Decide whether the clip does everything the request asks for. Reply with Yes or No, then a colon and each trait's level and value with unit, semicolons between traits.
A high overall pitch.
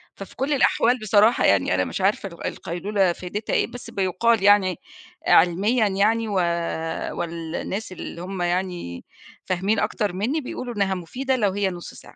Yes: high, 195 Hz